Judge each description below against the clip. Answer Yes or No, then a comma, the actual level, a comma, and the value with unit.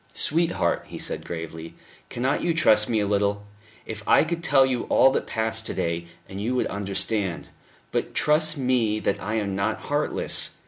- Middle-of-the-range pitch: No, low, 110 Hz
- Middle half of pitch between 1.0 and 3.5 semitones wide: No, average, 4.9 semitones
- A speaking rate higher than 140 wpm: Yes, average, 175 wpm